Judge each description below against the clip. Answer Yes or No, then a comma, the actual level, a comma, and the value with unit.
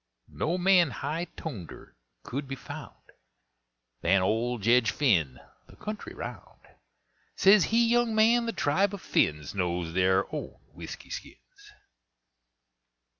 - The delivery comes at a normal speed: No, slow, 125 wpm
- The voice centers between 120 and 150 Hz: Yes, medium, 140 Hz